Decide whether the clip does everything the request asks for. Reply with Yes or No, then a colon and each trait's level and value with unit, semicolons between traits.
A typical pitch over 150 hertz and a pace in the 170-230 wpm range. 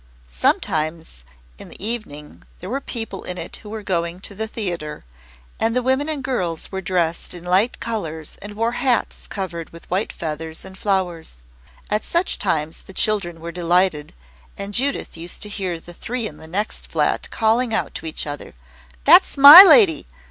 Yes: high, 190 Hz; average, 175 wpm